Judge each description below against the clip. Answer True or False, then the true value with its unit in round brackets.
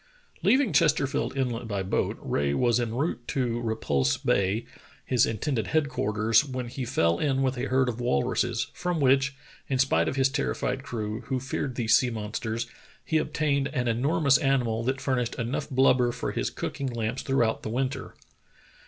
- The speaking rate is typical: True (170 wpm)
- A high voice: False (125 Hz)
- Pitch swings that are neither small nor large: True (3.1 semitones)